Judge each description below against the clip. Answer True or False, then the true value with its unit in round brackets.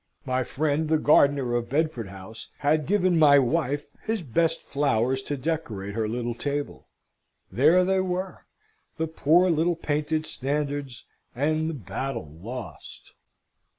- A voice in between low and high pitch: True (145 Hz)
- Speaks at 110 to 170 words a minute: True (135 wpm)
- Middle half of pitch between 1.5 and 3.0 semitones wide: False (4.4 semitones)